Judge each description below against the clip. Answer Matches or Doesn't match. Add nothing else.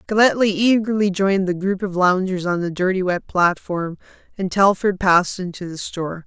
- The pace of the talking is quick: Doesn't match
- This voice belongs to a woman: Matches